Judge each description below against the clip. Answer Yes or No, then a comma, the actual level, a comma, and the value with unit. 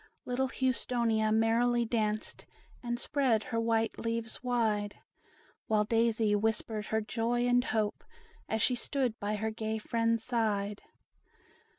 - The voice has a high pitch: Yes, high, 225 Hz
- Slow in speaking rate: Yes, slow, 125 wpm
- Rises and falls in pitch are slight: Yes, narrow, 1.8 semitones